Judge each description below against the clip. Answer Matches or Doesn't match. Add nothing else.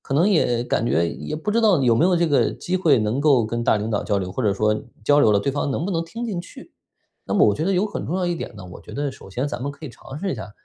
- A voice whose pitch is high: Doesn't match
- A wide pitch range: Matches